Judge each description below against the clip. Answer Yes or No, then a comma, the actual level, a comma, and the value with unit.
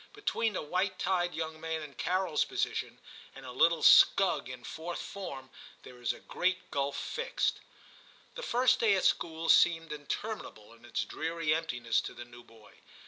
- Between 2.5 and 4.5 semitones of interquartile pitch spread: No, wide, 5.6 semitones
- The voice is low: No, medium, 165 Hz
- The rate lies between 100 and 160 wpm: No, average, 175 wpm